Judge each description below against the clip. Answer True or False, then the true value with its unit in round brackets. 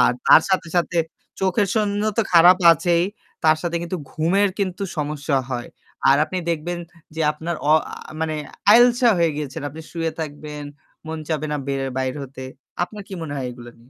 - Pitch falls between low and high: True (160 Hz)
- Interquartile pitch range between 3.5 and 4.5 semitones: True (3.8 semitones)